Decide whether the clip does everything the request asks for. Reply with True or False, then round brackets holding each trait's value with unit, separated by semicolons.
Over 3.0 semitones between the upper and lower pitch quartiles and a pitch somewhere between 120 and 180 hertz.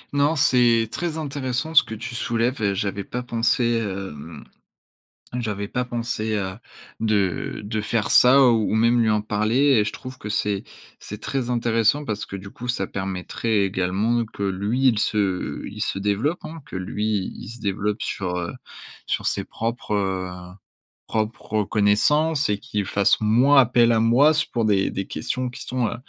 False (3.5 semitones; 110 Hz)